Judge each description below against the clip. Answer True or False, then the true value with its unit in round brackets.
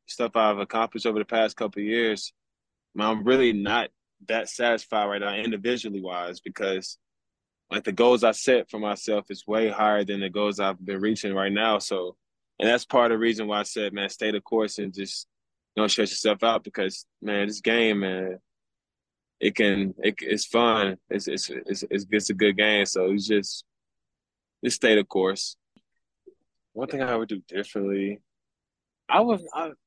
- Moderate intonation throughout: False (2.2 semitones)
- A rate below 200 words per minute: True (190 wpm)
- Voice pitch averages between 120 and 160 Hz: False (105 Hz)